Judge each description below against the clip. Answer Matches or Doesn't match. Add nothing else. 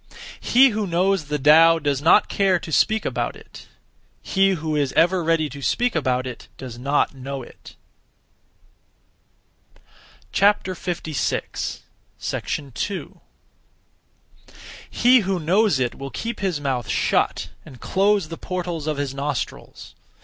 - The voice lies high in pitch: Doesn't match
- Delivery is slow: Matches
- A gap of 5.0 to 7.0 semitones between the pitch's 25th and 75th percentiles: Matches